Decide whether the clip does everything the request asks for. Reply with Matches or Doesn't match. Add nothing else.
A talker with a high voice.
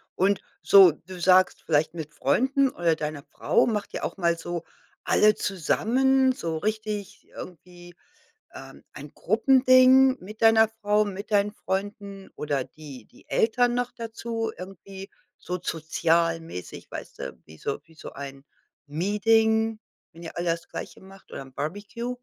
Matches